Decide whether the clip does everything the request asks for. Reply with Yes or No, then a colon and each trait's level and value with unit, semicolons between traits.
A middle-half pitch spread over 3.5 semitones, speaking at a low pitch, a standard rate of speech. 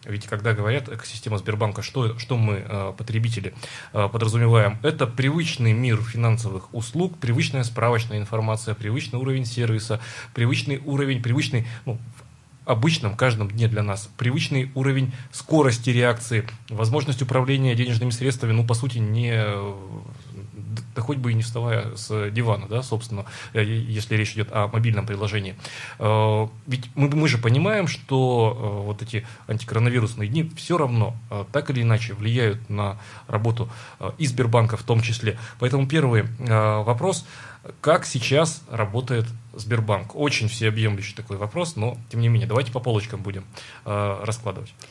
No: average, 2.9 semitones; low, 115 Hz; average, 135 wpm